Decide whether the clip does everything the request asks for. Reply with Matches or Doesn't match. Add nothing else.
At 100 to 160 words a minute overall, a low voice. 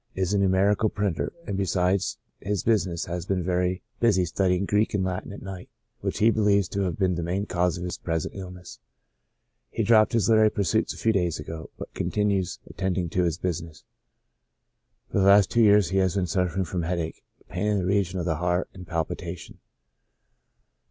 Doesn't match